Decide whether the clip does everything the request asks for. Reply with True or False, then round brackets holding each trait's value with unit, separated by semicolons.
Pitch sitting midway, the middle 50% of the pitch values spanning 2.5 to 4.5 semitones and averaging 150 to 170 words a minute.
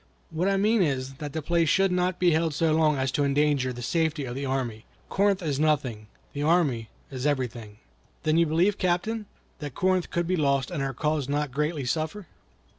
False (150 Hz; 4.2 semitones; 200 wpm)